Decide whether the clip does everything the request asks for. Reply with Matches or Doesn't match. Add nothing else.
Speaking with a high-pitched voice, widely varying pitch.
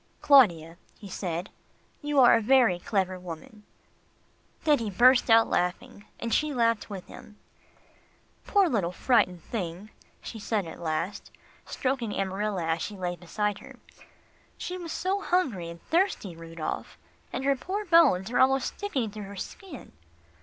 Matches